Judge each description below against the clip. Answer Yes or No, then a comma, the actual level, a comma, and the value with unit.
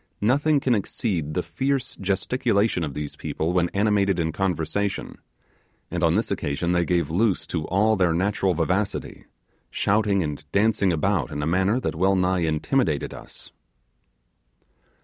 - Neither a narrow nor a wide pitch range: Yes, average, 4.1 semitones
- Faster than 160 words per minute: No, average, 150 wpm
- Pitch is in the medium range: No, very low, 95 Hz